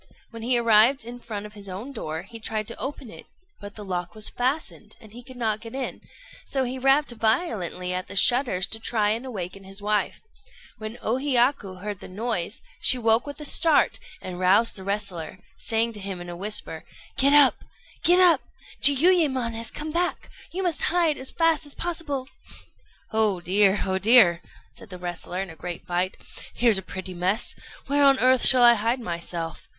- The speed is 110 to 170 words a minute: No, average, 195 wpm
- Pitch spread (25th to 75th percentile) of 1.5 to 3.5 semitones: No, average, 5.3 semitones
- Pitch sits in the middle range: No, high, 225 Hz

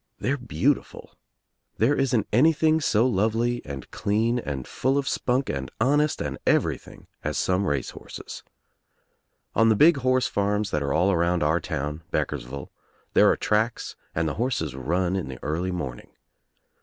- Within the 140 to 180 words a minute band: Yes, average, 160 wpm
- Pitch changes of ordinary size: No, wide, 8.5 semitones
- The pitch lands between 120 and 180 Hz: No, low, 105 Hz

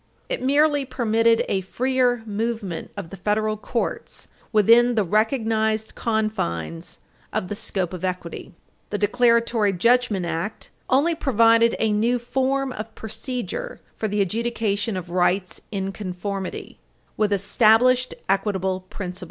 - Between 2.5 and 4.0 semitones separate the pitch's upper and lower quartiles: Yes, average, 3.6 semitones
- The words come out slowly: Yes, slow, 125 wpm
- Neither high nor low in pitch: No, high, 220 Hz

